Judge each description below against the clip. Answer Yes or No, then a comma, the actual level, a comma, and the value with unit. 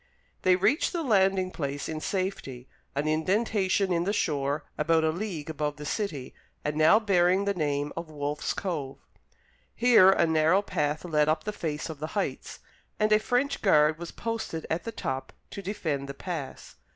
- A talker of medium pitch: Yes, medium, 165 Hz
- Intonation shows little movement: No, average, 4.9 semitones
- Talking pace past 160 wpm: Yes, average, 175 wpm